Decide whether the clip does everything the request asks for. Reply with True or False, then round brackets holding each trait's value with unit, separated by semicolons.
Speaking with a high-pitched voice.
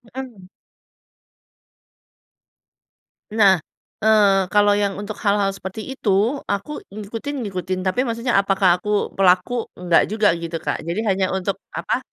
True (200 Hz)